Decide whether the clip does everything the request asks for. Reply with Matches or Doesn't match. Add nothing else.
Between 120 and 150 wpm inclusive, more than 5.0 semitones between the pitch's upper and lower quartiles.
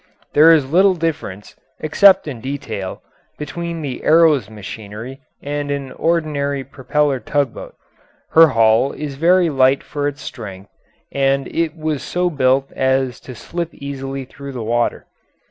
Doesn't match